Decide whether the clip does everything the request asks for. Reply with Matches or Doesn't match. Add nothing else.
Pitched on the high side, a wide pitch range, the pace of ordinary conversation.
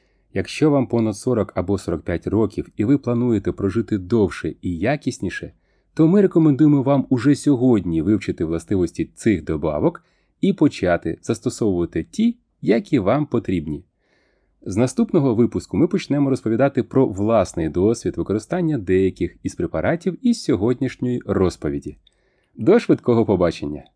Doesn't match